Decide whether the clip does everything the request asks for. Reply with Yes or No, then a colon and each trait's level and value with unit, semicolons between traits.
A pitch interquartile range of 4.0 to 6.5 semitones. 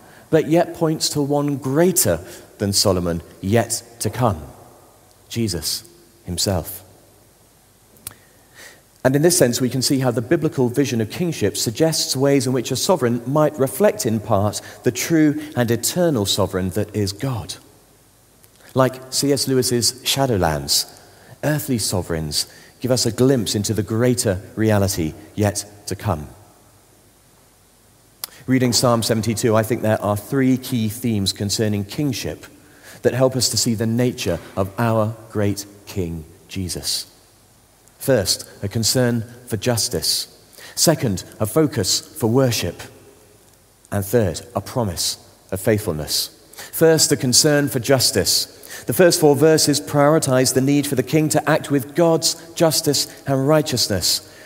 Yes: average, 4.8 semitones